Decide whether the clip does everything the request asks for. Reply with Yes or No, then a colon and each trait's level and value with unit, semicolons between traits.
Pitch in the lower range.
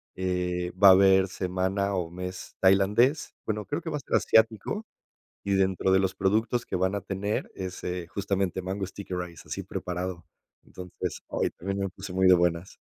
Yes: very low, 95 Hz